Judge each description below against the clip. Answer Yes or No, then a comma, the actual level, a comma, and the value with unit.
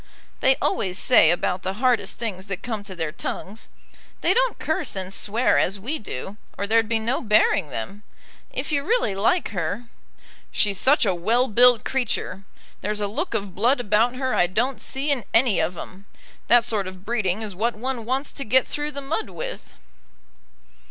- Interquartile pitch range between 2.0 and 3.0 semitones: No, average, 4.6 semitones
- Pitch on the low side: No, high, 220 Hz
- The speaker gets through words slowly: No, average, 190 wpm